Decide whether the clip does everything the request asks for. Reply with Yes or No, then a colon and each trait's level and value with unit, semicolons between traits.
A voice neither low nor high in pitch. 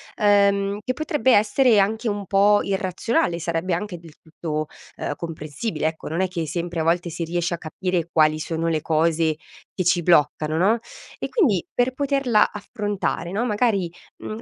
Yes: medium, 180 Hz